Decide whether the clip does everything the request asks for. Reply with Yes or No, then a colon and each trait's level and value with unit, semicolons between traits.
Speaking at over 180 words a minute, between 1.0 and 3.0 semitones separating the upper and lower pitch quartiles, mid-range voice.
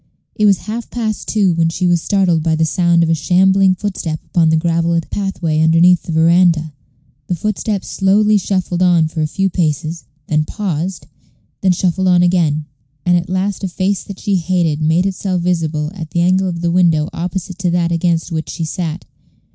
Yes: average, 190 wpm; narrow, 2.5 semitones; medium, 175 Hz